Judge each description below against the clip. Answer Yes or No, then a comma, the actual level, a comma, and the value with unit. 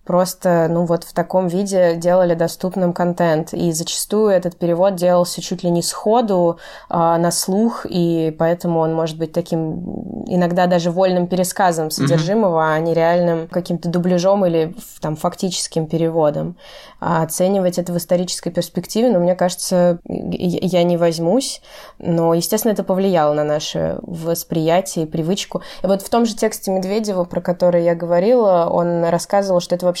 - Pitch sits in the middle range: Yes, medium, 175 Hz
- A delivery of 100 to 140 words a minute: No, average, 155 wpm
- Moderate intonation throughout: No, narrow, 2.0 semitones